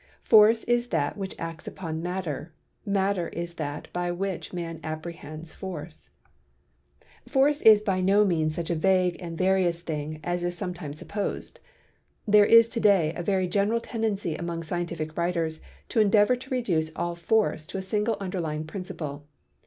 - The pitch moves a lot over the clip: No, average, 3.7 semitones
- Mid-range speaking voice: Yes, medium, 175 Hz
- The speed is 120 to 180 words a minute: Yes, average, 160 wpm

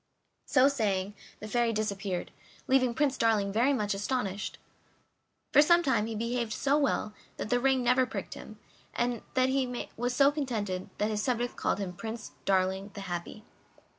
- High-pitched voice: Yes, high, 230 Hz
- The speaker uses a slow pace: No, average, 165 wpm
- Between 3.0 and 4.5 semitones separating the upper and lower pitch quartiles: Yes, average, 4.1 semitones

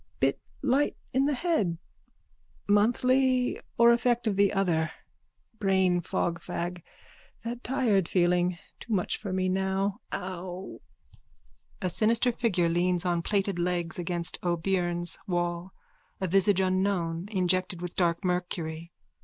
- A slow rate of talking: Yes, slow, 120 wpm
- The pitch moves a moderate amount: Yes, average, 3.0 semitones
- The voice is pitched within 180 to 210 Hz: Yes, medium, 185 Hz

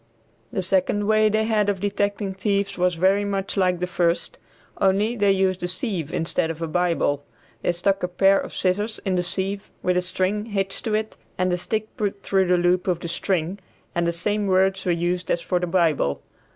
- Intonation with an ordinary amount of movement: No, narrow, 2.2 semitones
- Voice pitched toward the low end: No, high, 190 Hz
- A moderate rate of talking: No, fast, 210 wpm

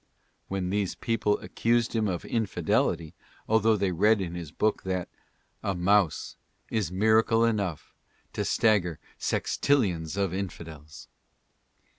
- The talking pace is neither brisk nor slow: No, slow, 120 wpm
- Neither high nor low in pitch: No, low, 100 Hz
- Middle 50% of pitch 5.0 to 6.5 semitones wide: No, average, 3.9 semitones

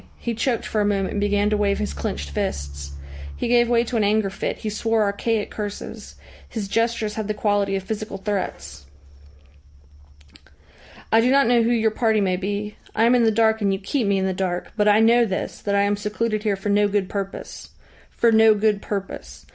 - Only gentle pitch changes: Yes, narrow, 2.2 semitones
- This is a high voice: Yes, high, 210 Hz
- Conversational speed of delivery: No, fast, 210 wpm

